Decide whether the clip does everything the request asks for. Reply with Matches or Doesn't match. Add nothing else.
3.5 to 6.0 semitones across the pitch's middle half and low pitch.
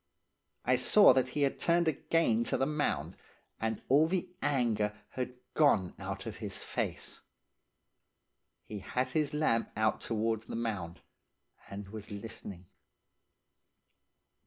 Matches